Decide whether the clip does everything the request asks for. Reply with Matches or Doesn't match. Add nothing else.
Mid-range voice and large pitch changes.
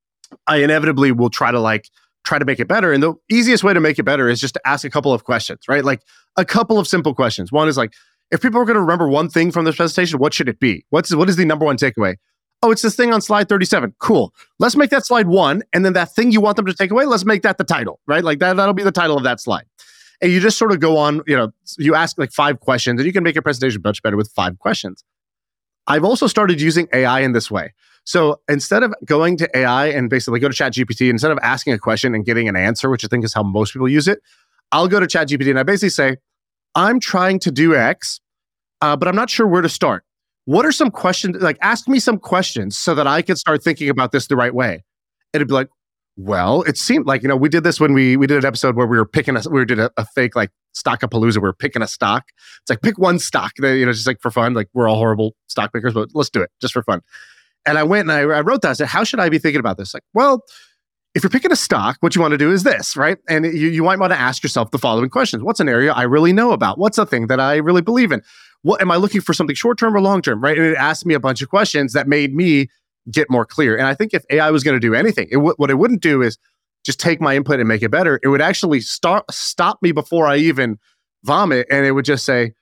Matches